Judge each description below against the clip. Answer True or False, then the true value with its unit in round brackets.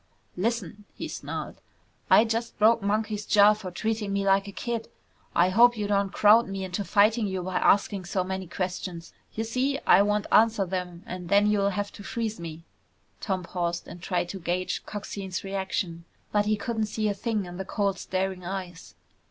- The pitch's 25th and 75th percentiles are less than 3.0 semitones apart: True (2.5 semitones)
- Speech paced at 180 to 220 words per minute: True (185 wpm)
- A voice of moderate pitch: False (200 Hz)